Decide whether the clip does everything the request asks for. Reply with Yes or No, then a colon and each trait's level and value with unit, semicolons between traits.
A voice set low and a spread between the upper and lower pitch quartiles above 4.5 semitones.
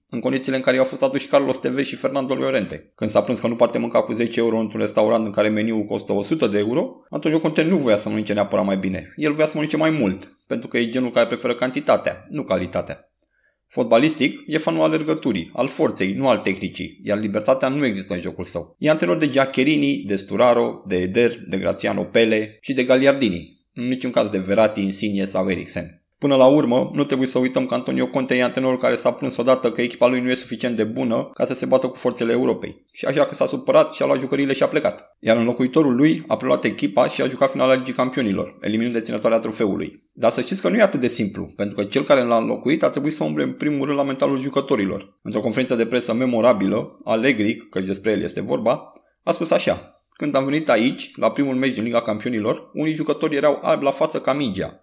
No: low, 120 Hz; average, 4.2 semitones